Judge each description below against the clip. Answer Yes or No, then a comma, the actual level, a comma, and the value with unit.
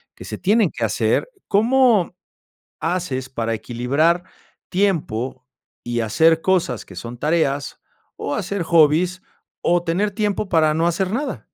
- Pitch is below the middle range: No, medium, 165 Hz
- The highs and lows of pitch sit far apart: Yes, wide, 6.6 semitones